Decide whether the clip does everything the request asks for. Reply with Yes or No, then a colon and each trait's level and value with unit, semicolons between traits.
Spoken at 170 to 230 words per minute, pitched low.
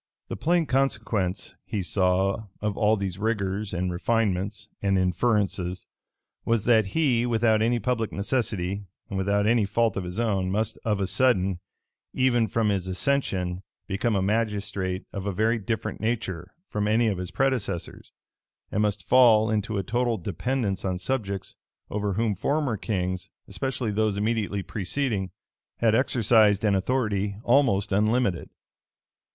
No: average, 145 wpm; low, 105 Hz